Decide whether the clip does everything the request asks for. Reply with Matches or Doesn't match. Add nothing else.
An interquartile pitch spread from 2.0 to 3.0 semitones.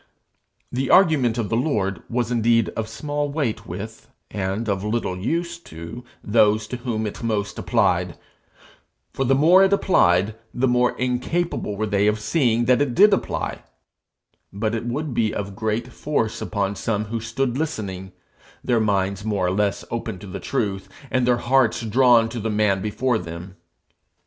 Doesn't match